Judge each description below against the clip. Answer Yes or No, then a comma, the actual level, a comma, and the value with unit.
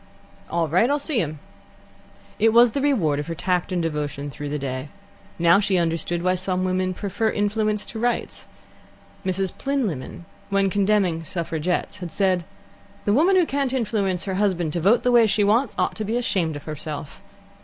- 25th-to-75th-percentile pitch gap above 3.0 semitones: Yes, average, 4.6 semitones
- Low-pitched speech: No, medium, 185 Hz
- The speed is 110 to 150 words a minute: No, average, 180 wpm